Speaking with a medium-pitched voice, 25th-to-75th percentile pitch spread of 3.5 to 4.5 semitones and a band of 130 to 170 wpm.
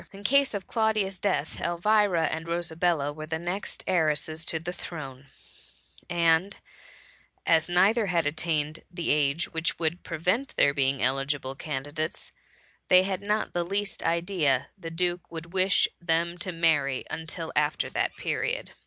No: medium, 170 Hz; average, 3.1 semitones; average, 150 wpm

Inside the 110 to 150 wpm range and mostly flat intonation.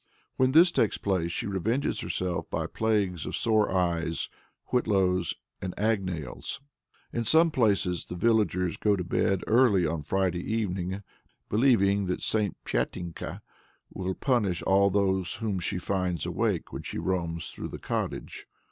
No: average, 140 wpm; average, 3.5 semitones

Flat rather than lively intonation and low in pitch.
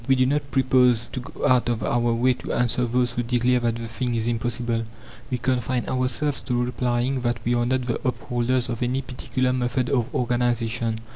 Yes: narrow, 1.2 semitones; low, 125 Hz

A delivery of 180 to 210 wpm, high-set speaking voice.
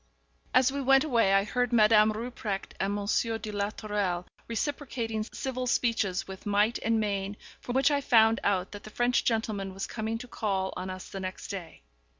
Yes: average, 185 wpm; high, 215 Hz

